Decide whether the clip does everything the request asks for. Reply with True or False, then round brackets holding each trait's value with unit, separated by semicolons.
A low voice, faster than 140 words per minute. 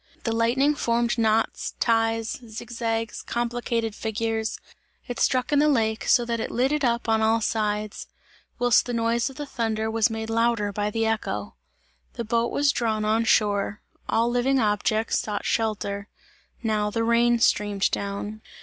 False (225 Hz; 160 wpm)